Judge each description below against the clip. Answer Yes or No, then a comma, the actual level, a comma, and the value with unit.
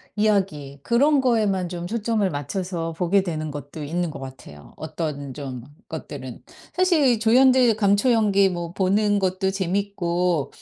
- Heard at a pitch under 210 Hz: Yes, high, 190 Hz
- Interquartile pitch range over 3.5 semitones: Yes, average, 5.0 semitones